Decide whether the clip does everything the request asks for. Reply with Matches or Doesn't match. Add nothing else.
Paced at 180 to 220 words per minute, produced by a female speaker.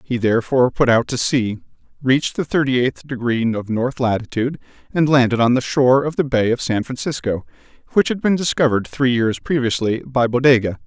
Doesn't match